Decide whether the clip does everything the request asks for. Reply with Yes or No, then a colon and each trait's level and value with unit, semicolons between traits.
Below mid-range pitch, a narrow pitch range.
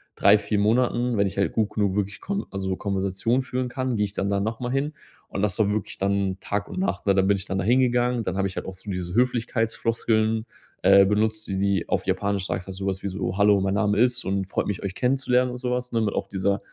No: low, 105 Hz; average, 3.7 semitones